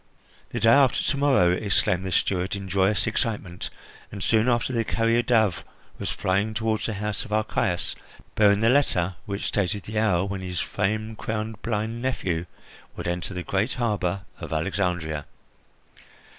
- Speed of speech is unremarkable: Yes, average, 160 wpm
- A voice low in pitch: Yes, low, 105 Hz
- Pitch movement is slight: No, average, 3.3 semitones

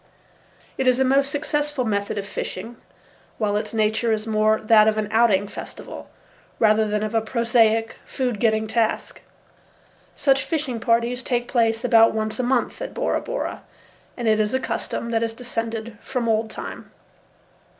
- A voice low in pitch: No, high, 225 Hz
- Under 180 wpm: Yes, average, 165 wpm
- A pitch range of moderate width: No, narrow, 2.2 semitones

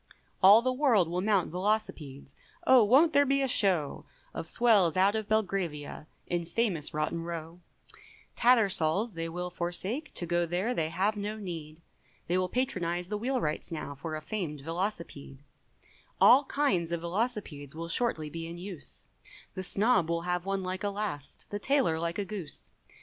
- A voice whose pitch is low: No, medium, 180 Hz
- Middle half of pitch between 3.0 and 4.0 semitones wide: No, average, 4.6 semitones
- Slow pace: No, average, 170 wpm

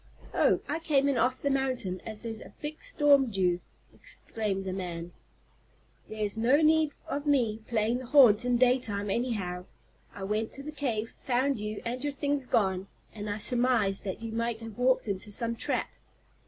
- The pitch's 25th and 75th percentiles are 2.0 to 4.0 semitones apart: No, average, 4.6 semitones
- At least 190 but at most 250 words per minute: No, average, 180 wpm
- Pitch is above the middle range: Yes, high, 230 Hz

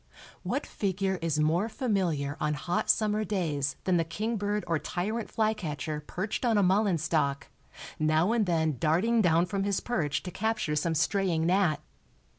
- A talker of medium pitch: Yes, medium, 180 Hz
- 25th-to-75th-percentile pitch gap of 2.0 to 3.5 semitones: No, average, 4.8 semitones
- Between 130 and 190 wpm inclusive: Yes, average, 160 wpm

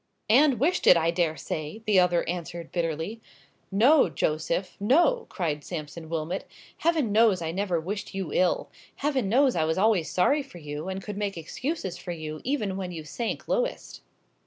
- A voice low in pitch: No, medium, 185 Hz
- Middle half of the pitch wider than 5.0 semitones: Yes, wide, 5.6 semitones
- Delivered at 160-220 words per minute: Yes, average, 170 wpm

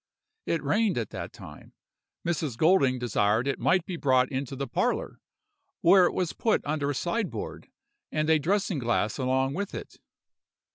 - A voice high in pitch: No, medium, 145 Hz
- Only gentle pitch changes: No, wide, 5.5 semitones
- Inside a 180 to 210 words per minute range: No, average, 160 wpm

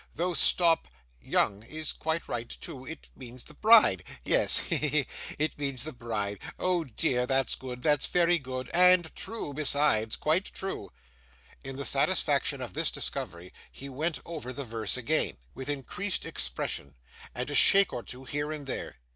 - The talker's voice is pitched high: No, medium, 140 Hz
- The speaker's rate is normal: Yes, average, 170 wpm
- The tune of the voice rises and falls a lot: No, average, 4.6 semitones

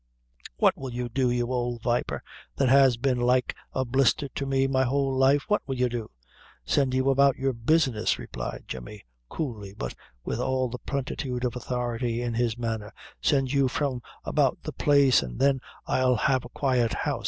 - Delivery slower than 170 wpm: No, average, 185 wpm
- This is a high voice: No, low, 125 Hz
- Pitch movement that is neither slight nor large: No, narrow, 2.0 semitones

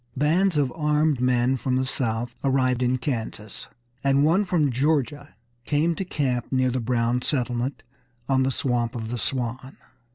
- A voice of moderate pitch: No, low, 130 Hz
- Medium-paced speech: Yes, average, 160 wpm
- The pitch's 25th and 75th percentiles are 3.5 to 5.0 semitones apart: No, average, 3.1 semitones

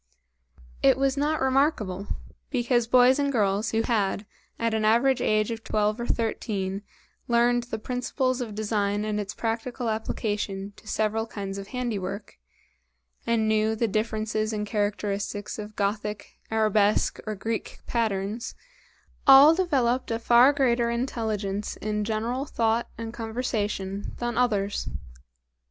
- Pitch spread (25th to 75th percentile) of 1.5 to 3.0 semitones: Yes, narrow, 2.5 semitones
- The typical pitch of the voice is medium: No, high, 220 Hz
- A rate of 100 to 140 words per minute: Yes, slow, 135 wpm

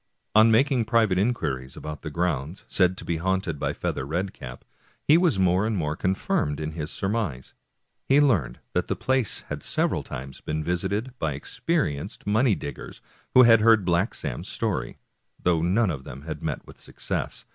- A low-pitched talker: Yes, very low, 90 Hz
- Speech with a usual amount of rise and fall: No, wide, 6.6 semitones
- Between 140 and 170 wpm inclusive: No, average, 180 wpm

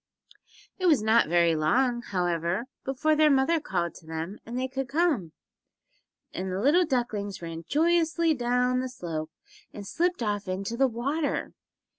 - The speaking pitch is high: Yes, high, 240 Hz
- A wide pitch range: Yes, wide, 7.5 semitones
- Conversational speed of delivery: Yes, average, 155 wpm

